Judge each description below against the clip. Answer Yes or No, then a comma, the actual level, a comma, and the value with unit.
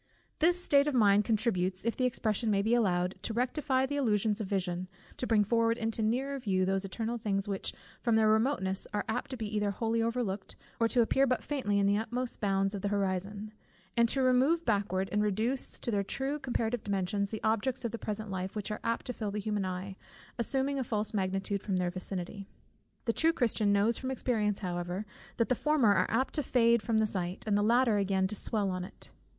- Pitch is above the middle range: Yes, high, 215 Hz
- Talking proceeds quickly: Yes, fast, 215 wpm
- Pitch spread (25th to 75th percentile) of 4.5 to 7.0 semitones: No, average, 3.4 semitones